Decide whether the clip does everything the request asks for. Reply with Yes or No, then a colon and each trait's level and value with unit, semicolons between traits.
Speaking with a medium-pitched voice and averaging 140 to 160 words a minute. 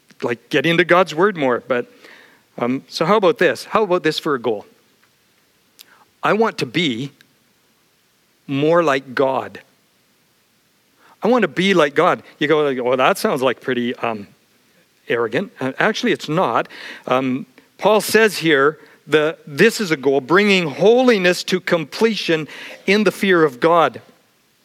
Yes: medium, 165 Hz; average, 150 wpm